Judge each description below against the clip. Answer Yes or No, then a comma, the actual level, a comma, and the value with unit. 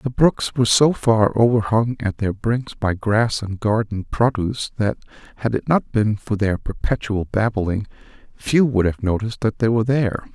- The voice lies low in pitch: Yes, low, 110 Hz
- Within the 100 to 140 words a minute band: No, average, 180 wpm